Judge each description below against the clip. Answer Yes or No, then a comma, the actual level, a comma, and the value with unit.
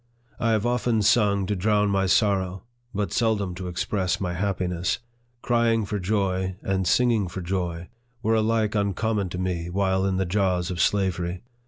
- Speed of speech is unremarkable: Yes, average, 170 wpm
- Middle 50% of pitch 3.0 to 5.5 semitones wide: No, narrow, 2.6 semitones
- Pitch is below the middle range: Yes, very low, 95 Hz